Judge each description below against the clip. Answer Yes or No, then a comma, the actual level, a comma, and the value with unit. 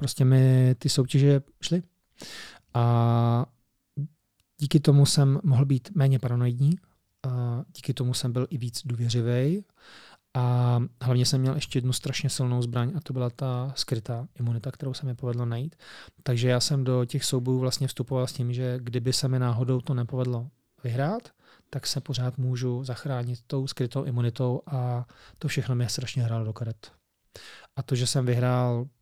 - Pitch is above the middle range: No, low, 130 Hz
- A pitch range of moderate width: No, narrow, 2.0 semitones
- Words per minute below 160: No, average, 165 wpm